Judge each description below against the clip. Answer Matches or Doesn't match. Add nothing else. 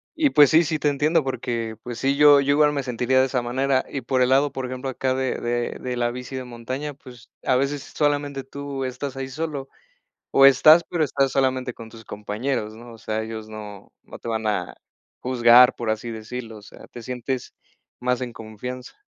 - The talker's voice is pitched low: Matches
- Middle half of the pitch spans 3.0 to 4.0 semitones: Doesn't match